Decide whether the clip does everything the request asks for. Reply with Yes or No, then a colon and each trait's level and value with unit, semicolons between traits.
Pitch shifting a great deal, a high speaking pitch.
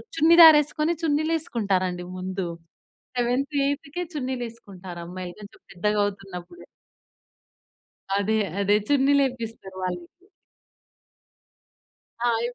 Yes: wide, 7.3 semitones; high, 225 Hz